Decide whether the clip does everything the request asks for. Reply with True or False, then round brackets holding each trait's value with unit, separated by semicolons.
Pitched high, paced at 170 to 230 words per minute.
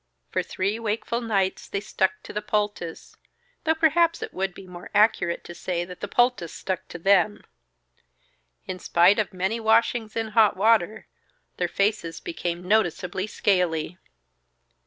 False (200 Hz; 150 wpm)